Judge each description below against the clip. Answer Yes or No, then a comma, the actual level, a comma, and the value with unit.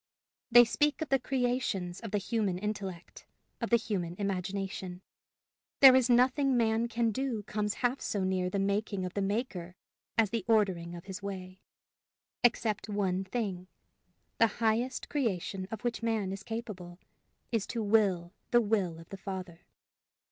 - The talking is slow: No, average, 155 wpm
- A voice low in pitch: No, high, 205 Hz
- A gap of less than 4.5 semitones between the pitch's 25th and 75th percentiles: Yes, average, 3.6 semitones